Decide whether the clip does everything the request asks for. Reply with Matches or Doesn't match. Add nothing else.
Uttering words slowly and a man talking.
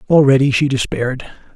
Matches